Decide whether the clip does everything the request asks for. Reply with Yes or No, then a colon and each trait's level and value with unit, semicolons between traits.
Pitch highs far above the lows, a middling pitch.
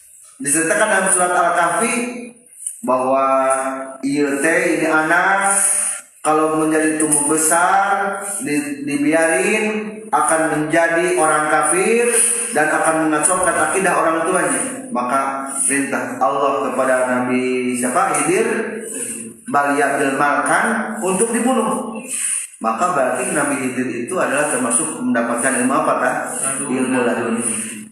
Yes: wide, 6.7 semitones; medium, 155 Hz